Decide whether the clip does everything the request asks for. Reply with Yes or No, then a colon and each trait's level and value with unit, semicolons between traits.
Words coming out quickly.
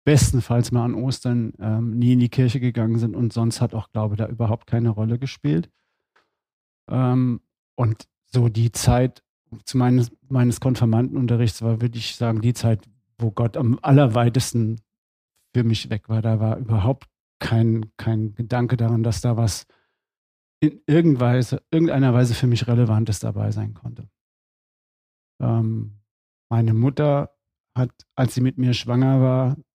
No: average, 150 wpm